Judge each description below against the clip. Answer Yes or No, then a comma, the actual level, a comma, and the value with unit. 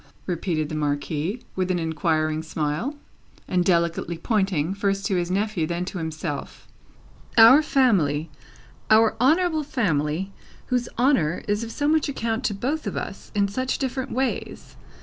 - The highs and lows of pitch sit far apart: Yes, wide, 7.3 semitones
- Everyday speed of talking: Yes, average, 150 wpm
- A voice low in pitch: No, high, 195 Hz